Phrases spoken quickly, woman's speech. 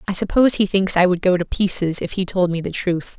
Yes: fast, 285 wpm; female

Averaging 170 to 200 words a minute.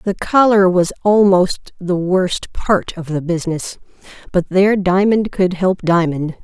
No: average, 150 wpm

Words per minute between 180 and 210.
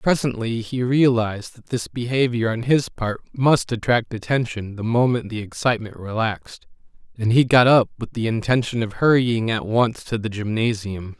No: average, 165 wpm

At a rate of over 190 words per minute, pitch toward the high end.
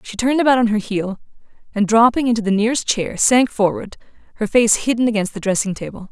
Yes: fast, 205 wpm; high, 220 Hz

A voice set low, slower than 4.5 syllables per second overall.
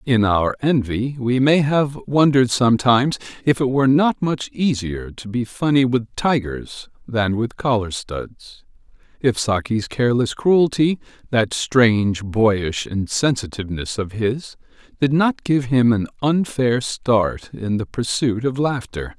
Yes: low, 125 Hz; 4.1 syllables/s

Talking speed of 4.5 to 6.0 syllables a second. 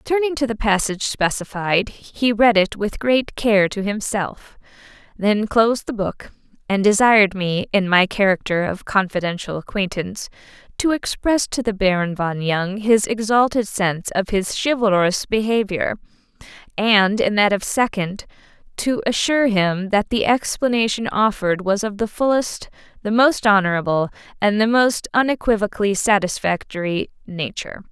Yes: 4.8 syllables/s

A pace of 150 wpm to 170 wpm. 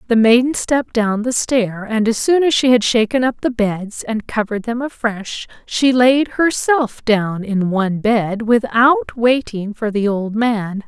No: average, 180 wpm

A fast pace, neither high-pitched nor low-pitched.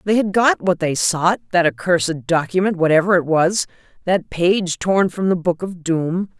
No: average, 190 wpm; medium, 175 Hz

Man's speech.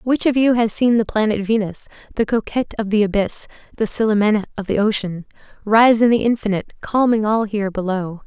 No: female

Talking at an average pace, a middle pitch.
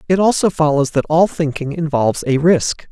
Yes: average, 185 wpm; medium, 155 Hz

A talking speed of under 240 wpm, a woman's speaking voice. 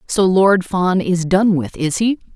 Yes: fast, 205 wpm; female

